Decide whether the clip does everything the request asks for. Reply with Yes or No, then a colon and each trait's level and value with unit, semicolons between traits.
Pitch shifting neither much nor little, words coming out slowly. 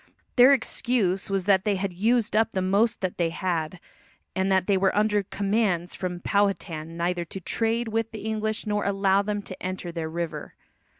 No: average, 3.0 semitones; average, 190 wpm